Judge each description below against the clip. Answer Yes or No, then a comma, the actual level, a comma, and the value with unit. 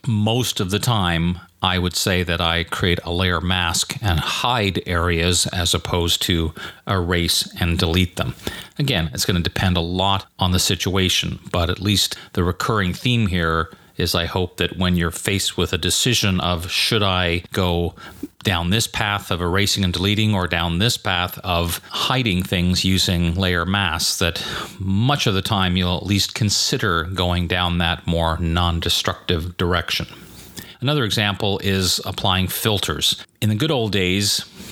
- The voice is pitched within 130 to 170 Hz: No, very low, 90 Hz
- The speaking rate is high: No, average, 165 wpm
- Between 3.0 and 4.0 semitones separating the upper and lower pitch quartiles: No, narrow, 2.6 semitones